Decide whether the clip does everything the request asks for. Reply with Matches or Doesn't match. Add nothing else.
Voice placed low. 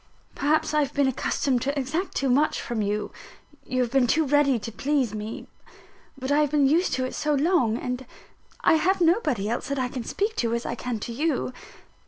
Doesn't match